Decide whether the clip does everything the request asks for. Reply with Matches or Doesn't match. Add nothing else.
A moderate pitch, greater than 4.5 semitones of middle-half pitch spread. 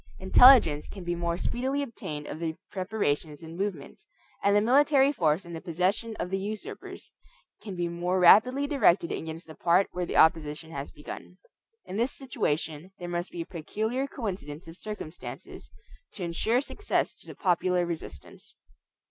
Matches